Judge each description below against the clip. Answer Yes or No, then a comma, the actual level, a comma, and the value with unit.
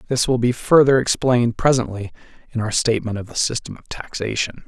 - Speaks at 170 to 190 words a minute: Yes, average, 180 wpm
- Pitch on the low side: Yes, low, 120 Hz